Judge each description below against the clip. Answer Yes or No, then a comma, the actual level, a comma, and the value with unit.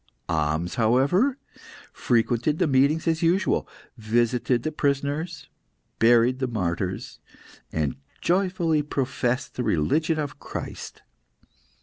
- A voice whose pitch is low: Yes, low, 130 Hz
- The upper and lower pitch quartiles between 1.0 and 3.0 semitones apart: No, wide, 5.5 semitones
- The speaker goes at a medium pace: No, slow, 100 wpm